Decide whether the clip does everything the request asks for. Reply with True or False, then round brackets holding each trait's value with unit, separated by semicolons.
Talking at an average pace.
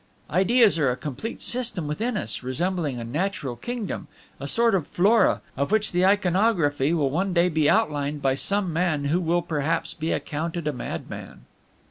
True (170 wpm)